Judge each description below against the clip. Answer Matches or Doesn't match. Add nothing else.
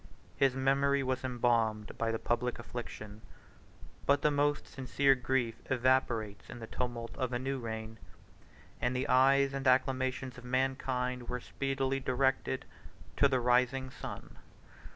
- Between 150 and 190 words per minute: Doesn't match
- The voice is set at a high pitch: Doesn't match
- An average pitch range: Doesn't match